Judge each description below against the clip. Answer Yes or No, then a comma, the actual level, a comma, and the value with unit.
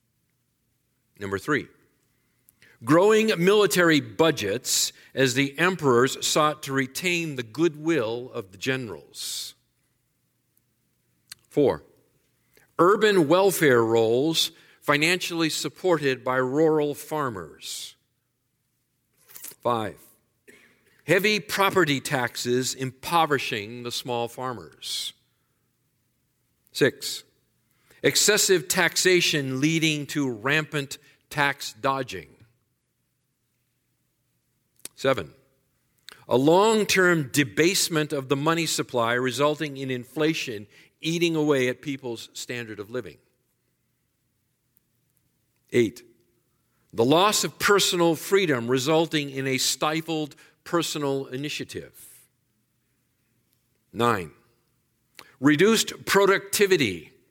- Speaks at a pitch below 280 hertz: Yes, low, 135 Hz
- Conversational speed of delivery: No, slow, 80 wpm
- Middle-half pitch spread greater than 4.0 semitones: Yes, average, 4.6 semitones